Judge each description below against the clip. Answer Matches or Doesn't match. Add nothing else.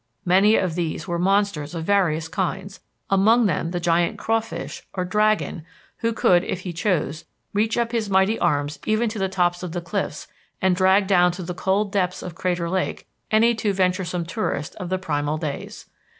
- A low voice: Doesn't match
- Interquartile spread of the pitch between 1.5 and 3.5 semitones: Matches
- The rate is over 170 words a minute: Matches